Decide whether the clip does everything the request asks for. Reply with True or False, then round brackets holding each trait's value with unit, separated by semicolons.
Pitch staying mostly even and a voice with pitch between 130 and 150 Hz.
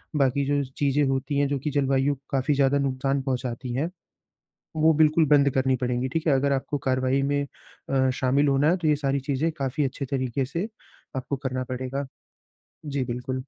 True (1.7 semitones; 135 Hz)